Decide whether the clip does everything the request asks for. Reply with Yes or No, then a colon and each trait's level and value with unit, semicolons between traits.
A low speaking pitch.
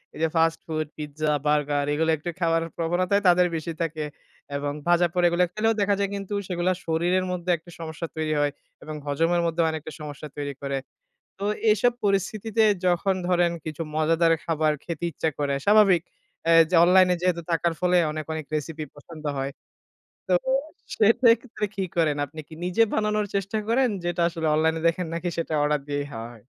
No: medium, 165 Hz